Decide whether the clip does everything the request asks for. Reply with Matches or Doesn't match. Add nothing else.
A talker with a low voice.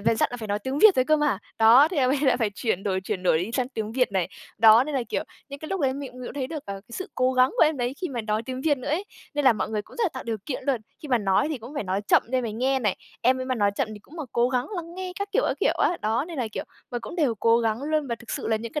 Doesn't match